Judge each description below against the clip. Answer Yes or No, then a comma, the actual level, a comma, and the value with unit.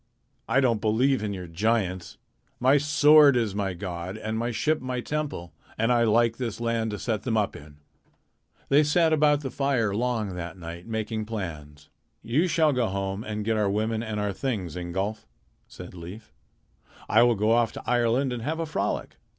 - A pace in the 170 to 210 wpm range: Yes, average, 185 wpm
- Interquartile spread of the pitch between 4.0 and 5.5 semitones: Yes, average, 4.3 semitones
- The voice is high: No, low, 110 Hz